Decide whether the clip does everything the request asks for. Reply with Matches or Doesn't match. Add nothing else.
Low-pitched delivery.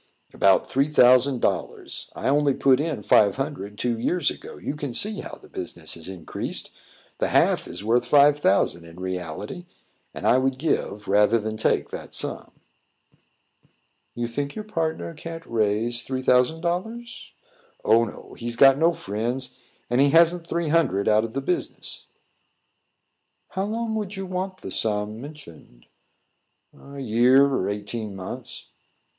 Matches